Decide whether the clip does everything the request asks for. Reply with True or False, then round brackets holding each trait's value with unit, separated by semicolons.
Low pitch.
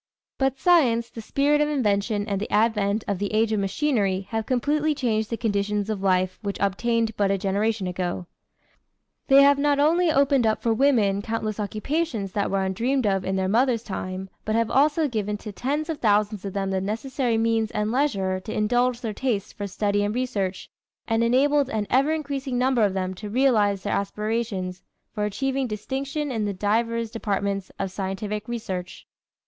False (220 Hz)